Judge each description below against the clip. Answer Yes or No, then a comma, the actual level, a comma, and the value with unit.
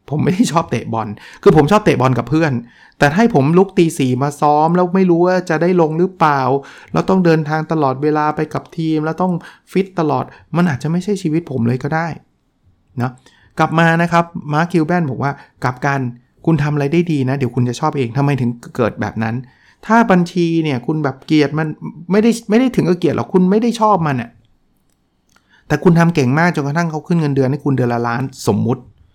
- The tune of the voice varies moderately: Yes, average, 4.6 semitones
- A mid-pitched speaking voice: Yes, medium, 155 Hz